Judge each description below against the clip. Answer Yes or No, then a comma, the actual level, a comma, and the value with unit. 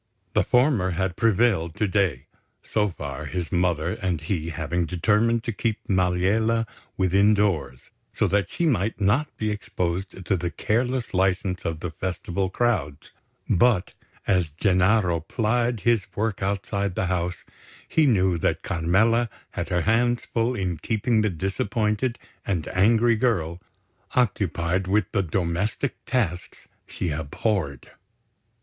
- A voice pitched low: Yes, very low, 95 Hz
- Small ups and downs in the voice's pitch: No, average, 4.2 semitones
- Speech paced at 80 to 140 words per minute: Yes, slow, 135 wpm